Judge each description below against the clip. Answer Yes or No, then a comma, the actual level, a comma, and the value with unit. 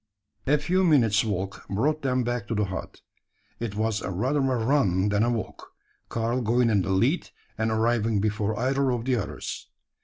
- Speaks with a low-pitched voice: Yes, low, 115 Hz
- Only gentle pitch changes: No, average, 3.6 semitones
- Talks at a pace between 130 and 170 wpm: No, average, 180 wpm